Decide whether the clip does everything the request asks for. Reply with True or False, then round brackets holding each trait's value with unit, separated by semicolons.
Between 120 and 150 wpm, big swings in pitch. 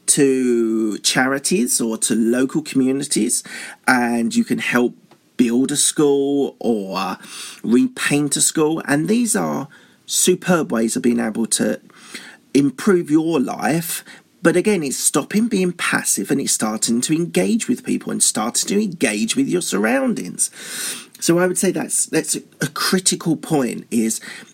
True (145 wpm; 7.1 semitones)